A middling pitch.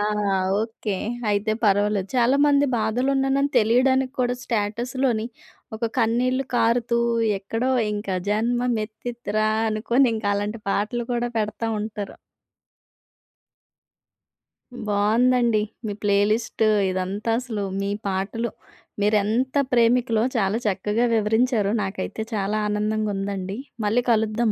No: high, 220 Hz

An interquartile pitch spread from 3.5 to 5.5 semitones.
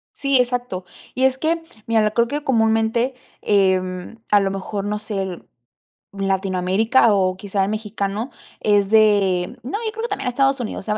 Yes: average, 4.1 semitones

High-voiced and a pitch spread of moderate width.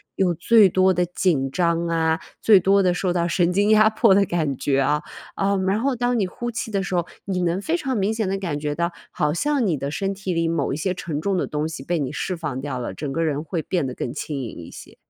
No: medium, 175 Hz; average, 4.4 semitones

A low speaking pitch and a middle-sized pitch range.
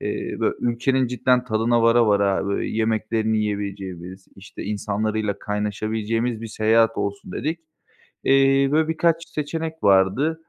Yes: low, 110 Hz; average, 4.1 semitones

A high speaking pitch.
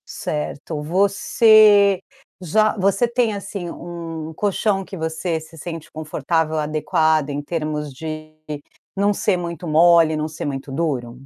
No: medium, 165 Hz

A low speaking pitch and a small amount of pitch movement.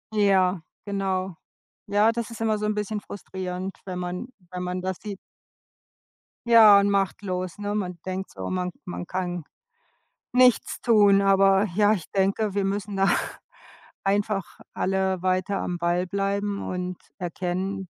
No: high, 195 Hz; narrow, 1.9 semitones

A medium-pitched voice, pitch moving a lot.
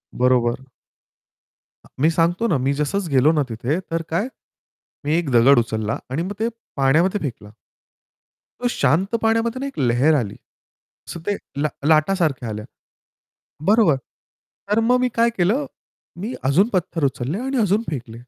Yes: medium, 160 Hz; wide, 7.6 semitones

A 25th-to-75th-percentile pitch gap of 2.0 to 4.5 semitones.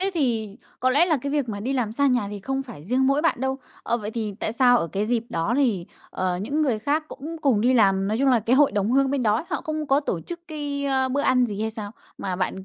No: average, 4.9 semitones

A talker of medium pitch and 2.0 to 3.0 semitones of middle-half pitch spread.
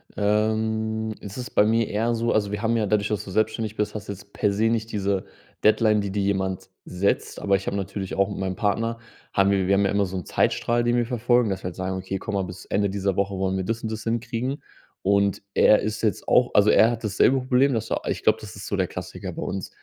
No: low, 105 Hz; narrow, 2.5 semitones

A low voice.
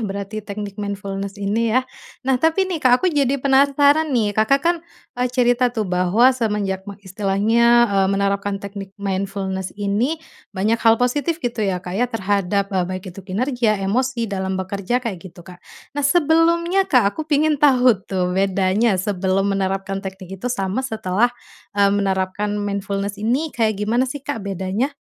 No: high, 205 Hz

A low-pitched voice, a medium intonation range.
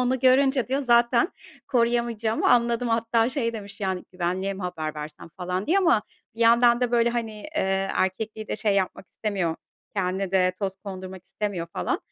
No: high, 215 Hz; average, 4.0 semitones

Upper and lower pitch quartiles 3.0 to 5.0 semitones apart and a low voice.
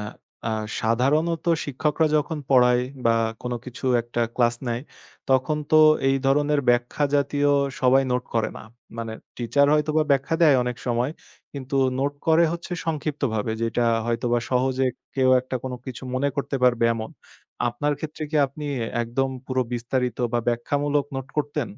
Yes: average, 3.3 semitones; low, 130 Hz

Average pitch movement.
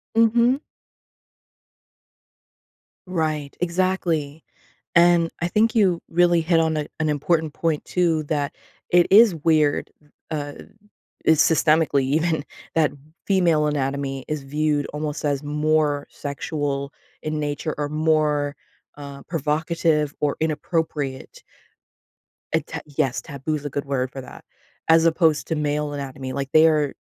No: narrow, 2.2 semitones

